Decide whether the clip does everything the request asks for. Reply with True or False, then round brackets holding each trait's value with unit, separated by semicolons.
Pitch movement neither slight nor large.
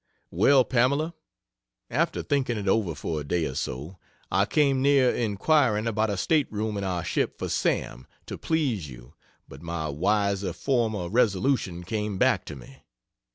False (6.5 semitones)